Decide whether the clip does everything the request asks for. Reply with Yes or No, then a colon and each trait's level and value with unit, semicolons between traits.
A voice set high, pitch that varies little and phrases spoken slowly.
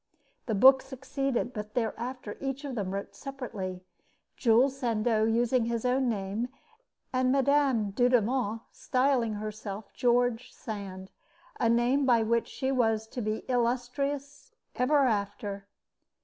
No: high, 240 Hz; average, 3.4 semitones; slow, 125 wpm